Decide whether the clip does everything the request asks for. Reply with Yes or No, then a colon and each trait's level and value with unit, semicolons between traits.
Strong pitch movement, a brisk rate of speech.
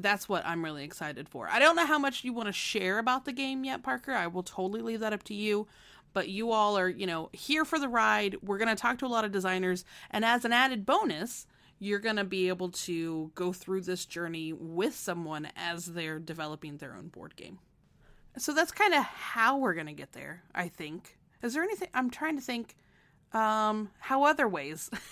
Yes: wide, 6.4 semitones; fast, 225 wpm